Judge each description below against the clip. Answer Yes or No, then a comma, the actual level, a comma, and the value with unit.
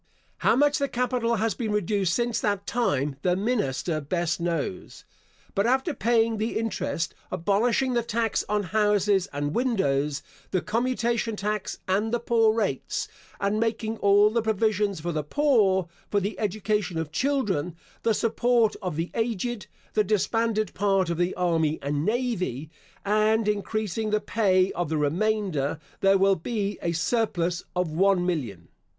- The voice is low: No, high, 205 Hz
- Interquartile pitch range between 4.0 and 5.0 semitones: Yes, average, 4.4 semitones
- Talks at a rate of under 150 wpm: No, average, 155 wpm